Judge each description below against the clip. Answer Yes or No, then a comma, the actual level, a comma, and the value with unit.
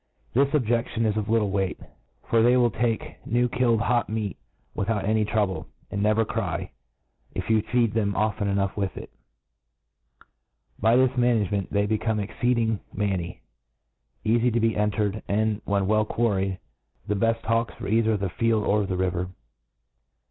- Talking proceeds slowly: No, average, 160 wpm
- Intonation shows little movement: Yes, narrow, 2.2 semitones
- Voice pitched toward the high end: No, low, 110 Hz